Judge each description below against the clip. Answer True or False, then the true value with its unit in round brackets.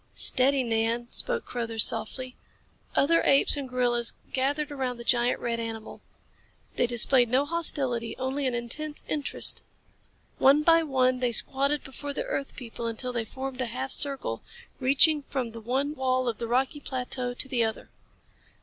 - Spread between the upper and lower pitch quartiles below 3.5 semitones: True (2.7 semitones)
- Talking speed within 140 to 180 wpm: True (160 wpm)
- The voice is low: False (255 Hz)